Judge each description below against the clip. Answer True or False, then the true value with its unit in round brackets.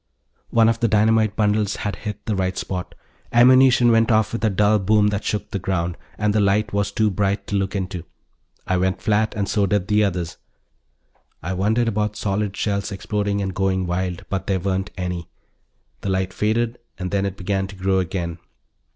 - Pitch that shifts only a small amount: True (2.2 semitones)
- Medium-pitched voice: False (100 Hz)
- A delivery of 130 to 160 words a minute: False (195 wpm)